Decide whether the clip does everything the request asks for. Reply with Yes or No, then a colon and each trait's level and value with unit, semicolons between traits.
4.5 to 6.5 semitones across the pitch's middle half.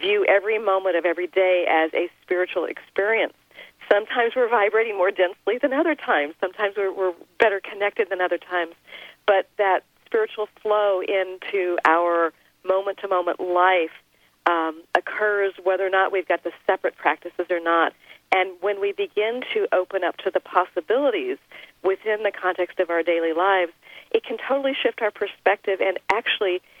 No: narrow, 2.6 semitones